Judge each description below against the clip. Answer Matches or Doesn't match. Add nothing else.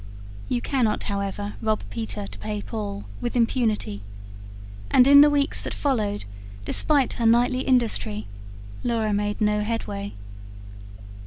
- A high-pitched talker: Matches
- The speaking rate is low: Matches